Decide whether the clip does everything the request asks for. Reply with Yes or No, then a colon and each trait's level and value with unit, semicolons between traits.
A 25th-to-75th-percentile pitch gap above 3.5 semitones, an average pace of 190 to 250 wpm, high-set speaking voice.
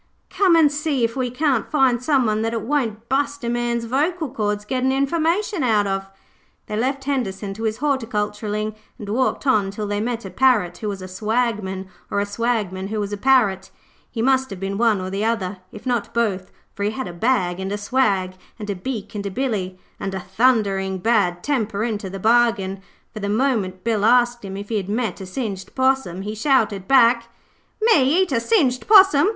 Yes: average, 4.6 semitones; average, 200 wpm; high, 225 Hz